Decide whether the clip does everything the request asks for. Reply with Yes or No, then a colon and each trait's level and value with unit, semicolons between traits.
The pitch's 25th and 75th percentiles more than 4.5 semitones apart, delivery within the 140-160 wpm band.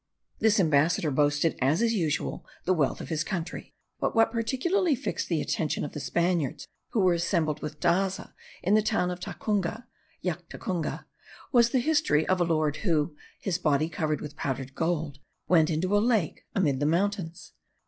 No: average, 5.0 semitones; average, 170 wpm